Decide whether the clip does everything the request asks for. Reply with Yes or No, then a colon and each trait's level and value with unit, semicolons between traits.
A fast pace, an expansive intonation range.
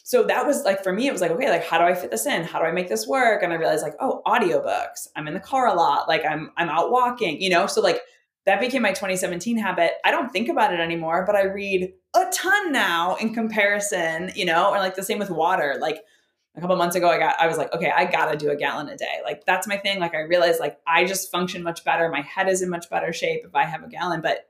No: fast, 285 wpm; average, 4.8 semitones